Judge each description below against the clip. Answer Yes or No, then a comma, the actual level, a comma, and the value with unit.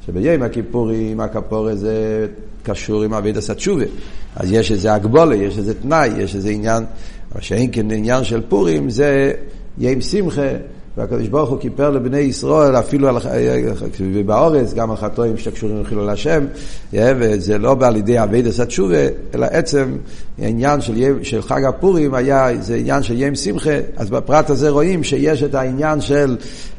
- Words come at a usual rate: No, fast, 160 wpm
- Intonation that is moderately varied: Yes, average, 4.6 semitones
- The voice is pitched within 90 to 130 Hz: Yes, low, 120 Hz